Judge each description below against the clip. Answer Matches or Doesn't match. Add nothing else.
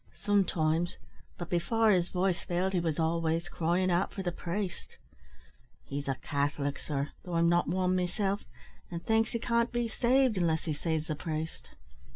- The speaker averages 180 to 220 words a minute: Doesn't match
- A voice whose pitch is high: Doesn't match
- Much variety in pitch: Doesn't match